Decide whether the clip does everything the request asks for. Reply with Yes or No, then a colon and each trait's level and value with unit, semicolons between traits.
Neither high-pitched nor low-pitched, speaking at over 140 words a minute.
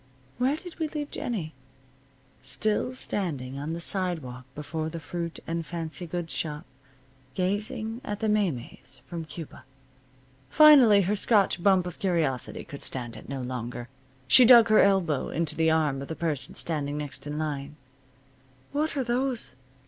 Yes: medium, 170 Hz; average, 155 wpm